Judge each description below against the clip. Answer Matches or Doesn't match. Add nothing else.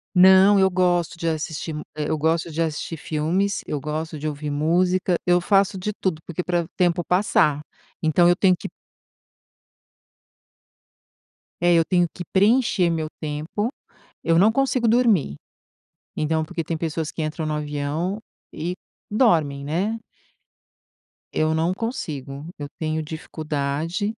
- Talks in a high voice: Doesn't match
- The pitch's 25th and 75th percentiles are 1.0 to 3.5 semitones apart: Matches